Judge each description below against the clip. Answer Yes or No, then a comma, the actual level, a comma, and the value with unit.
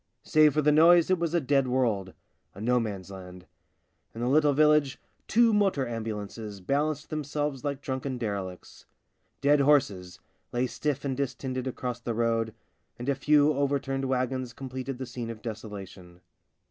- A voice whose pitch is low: Yes, low, 130 Hz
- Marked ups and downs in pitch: No, average, 4.3 semitones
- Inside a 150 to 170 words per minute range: Yes, average, 160 wpm